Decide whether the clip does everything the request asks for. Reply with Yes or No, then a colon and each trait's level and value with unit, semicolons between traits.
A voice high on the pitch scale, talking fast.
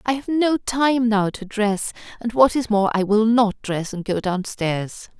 Yes: high, 220 Hz; fast, 220 wpm